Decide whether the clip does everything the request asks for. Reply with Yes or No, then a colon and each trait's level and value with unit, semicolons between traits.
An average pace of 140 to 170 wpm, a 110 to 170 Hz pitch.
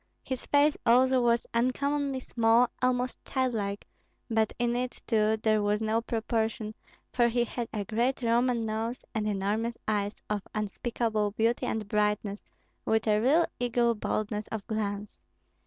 No: average, 145 wpm; high, 225 Hz